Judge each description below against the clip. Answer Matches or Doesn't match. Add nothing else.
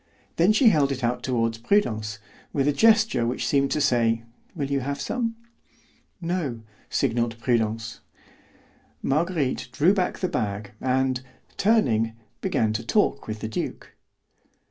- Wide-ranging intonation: Matches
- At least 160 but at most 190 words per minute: Doesn't match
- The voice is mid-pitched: Doesn't match